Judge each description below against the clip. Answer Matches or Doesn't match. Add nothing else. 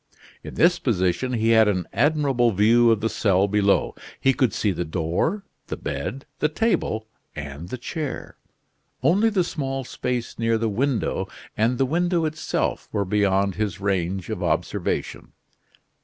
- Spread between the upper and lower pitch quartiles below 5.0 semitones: Doesn't match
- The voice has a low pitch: Matches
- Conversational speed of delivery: Matches